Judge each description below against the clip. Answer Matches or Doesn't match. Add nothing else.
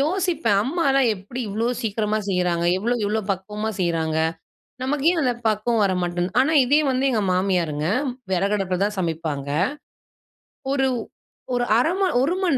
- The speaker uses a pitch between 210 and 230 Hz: Matches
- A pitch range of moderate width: Doesn't match